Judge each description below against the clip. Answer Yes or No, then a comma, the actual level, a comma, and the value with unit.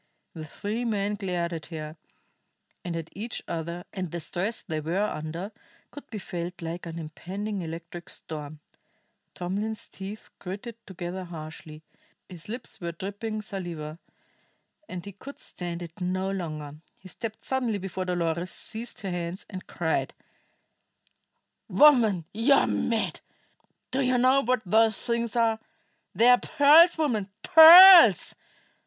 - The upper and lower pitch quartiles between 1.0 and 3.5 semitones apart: No, average, 4.8 semitones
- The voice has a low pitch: No, high, 190 Hz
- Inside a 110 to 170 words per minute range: Yes, average, 140 wpm